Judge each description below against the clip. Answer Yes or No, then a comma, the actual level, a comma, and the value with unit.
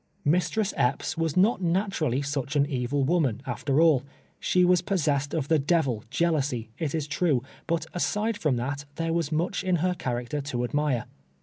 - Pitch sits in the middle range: Yes, medium, 150 Hz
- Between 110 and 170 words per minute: No, average, 185 wpm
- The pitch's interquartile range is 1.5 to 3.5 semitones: No, average, 4.0 semitones